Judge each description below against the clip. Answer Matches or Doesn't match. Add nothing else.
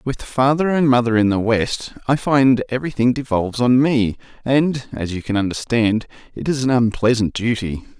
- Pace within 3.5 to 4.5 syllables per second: Doesn't match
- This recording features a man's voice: Matches